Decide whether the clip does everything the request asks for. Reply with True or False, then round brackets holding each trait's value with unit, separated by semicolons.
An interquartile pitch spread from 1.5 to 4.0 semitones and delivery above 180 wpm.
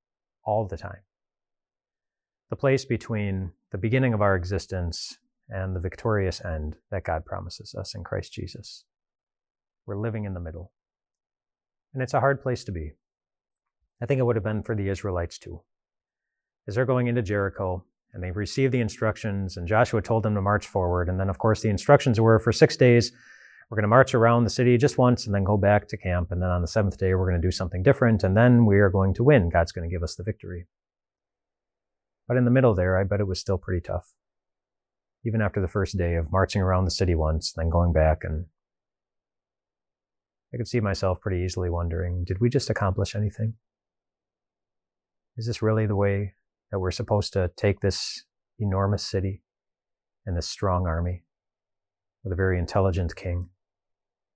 True (3.6 semitones; 190 wpm)